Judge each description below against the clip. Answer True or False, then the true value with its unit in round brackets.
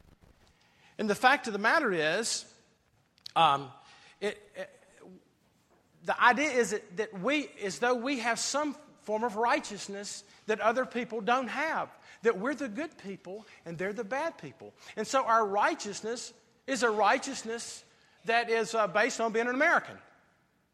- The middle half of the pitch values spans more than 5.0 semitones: False (4.1 semitones)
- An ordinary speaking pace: True (155 wpm)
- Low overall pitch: False (230 Hz)